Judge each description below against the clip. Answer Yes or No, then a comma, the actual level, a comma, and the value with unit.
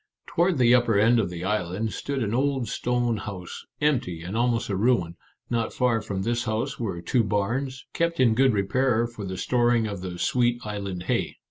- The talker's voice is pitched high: No, low, 115 Hz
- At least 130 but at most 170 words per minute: No, average, 195 wpm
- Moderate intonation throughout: Yes, average, 3.8 semitones